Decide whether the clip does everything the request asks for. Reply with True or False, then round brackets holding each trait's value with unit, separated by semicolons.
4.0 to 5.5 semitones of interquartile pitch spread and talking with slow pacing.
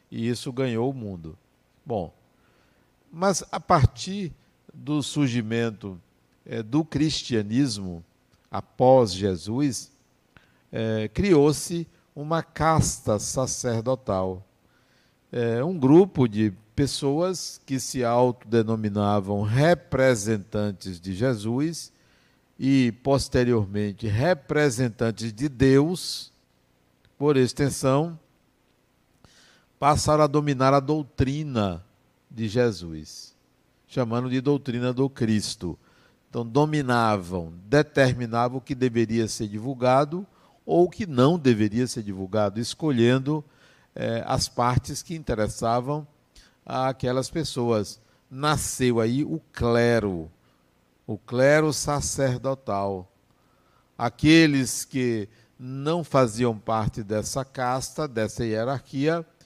True (4.8 semitones; 90 wpm)